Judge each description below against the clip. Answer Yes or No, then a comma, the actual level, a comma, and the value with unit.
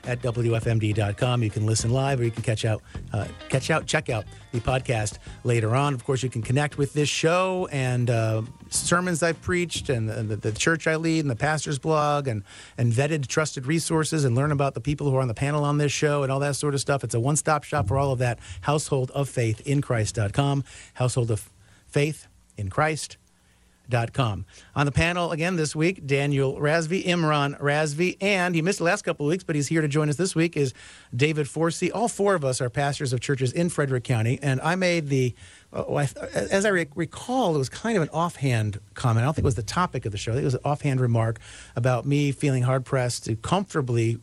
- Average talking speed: No, fast, 225 wpm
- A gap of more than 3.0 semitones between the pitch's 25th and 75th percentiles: Yes, average, 4.7 semitones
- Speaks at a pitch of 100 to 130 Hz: No, medium, 140 Hz